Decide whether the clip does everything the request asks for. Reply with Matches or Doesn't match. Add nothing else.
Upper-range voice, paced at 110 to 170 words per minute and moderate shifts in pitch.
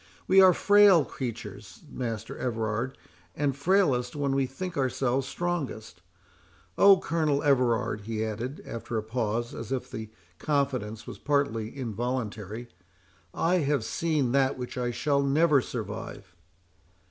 Doesn't match